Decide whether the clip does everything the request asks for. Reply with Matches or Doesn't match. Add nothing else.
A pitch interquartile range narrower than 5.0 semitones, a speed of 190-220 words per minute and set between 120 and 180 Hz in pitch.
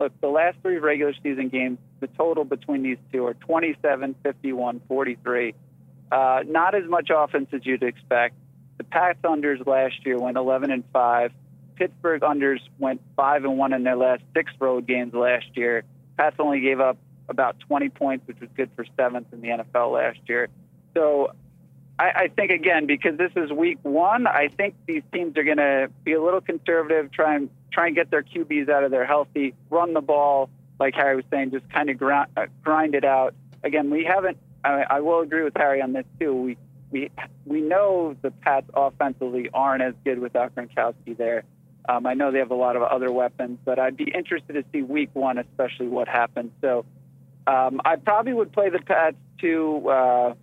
Matches